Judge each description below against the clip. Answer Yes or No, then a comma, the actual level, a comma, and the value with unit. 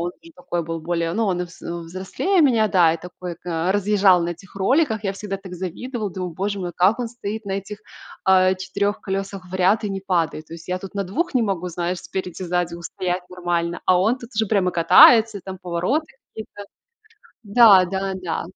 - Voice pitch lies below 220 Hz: Yes, high, 190 Hz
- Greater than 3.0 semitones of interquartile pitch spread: No, average, 2.7 semitones